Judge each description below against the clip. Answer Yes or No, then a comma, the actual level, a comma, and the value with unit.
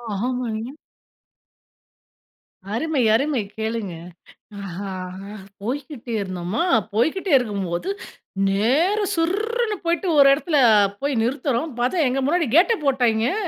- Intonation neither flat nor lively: No, wide, 6.5 semitones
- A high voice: Yes, very high, 265 Hz